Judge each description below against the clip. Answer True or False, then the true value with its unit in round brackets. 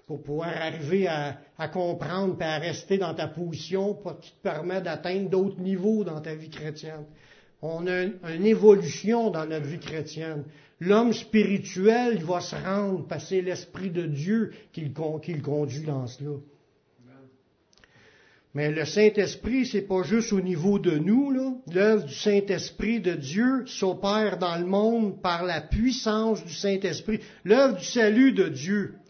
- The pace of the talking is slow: False (165 wpm)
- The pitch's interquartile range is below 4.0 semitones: False (4.7 semitones)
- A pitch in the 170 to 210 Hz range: True (185 Hz)